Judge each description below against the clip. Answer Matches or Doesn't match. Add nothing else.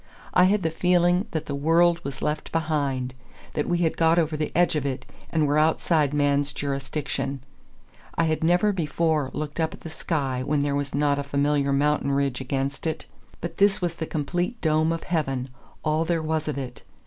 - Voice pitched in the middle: Matches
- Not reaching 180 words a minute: Doesn't match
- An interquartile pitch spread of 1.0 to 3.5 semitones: Matches